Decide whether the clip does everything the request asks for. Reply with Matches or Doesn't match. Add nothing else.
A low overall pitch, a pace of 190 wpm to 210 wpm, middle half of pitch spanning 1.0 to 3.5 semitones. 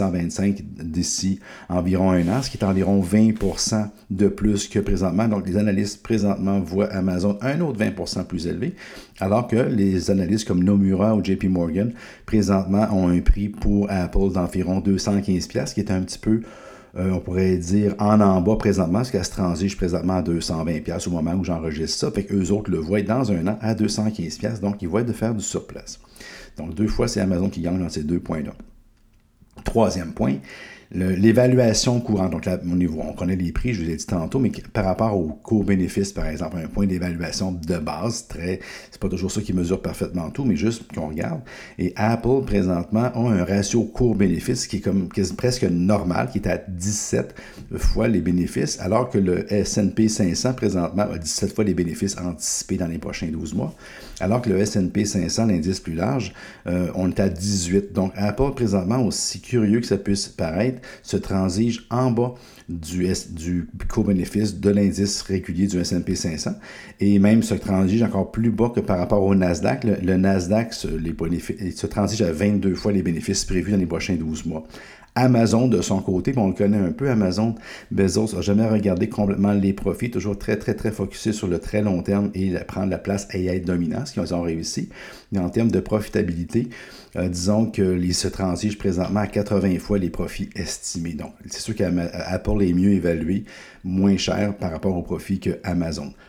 Matches